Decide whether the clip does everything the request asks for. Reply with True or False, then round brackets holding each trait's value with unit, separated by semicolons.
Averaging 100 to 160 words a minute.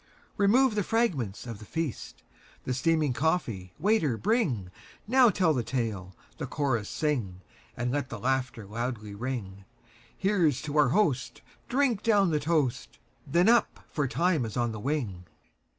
True (135 wpm)